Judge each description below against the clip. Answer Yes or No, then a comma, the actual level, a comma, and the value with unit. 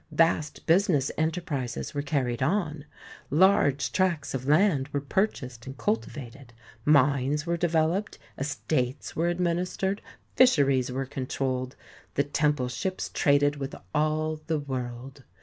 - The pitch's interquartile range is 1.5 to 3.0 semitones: No, average, 3.7 semitones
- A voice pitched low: No, medium, 145 Hz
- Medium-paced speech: No, slow, 120 wpm